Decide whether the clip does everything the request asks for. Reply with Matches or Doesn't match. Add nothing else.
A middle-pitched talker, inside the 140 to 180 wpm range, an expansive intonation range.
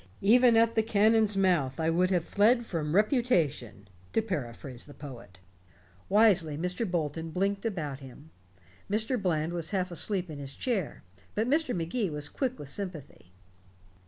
Matches